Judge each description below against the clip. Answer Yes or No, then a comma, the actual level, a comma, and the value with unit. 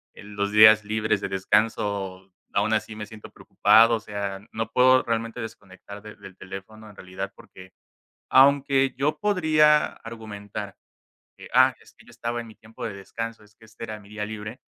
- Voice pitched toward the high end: No, low, 110 Hz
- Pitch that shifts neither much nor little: No, narrow, 2.1 semitones